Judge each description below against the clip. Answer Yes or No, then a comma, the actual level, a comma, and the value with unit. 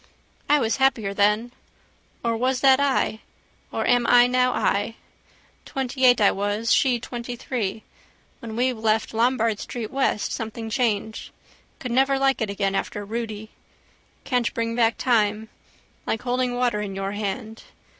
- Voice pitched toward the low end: No, high, 230 Hz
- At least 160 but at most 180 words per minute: No, average, 145 wpm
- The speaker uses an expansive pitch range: No, average, 2.8 semitones